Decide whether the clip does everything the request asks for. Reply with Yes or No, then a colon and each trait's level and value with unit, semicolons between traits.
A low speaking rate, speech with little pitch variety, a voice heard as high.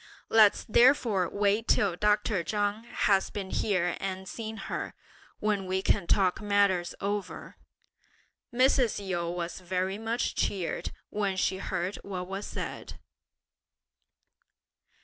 Yes: slow, 120 wpm; narrow, 2.2 semitones; high, 200 Hz